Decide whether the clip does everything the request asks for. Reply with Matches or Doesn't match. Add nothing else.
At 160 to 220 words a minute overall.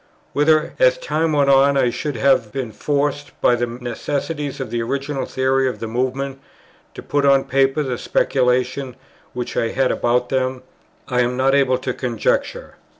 Matches